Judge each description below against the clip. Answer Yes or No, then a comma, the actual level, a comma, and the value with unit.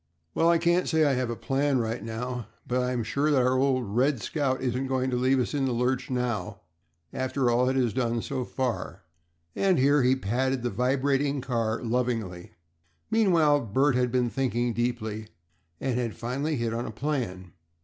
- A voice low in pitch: Yes, low, 125 Hz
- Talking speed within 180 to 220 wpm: Yes, average, 185 wpm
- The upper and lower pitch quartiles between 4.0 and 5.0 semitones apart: No, narrow, 2.4 semitones